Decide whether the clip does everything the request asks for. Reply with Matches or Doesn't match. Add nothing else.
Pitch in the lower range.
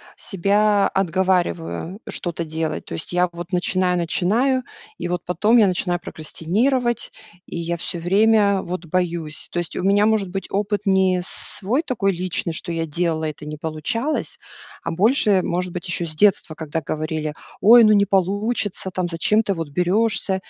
Doesn't match